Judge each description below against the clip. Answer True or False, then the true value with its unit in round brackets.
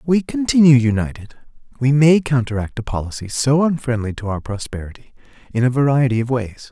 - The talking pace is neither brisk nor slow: True (170 wpm)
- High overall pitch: False (130 Hz)